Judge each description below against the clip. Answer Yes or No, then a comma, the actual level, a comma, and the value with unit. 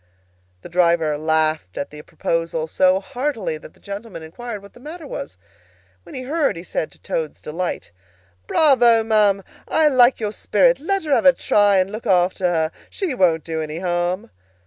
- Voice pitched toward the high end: Yes, high, 195 Hz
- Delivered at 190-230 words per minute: No, average, 180 wpm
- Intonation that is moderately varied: No, wide, 7.2 semitones